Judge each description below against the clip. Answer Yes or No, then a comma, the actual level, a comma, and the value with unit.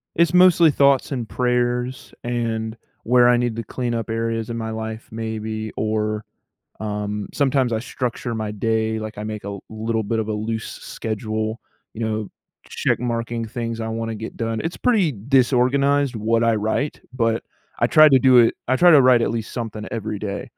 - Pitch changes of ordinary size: No, narrow, 2.1 semitones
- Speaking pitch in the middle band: No, low, 115 Hz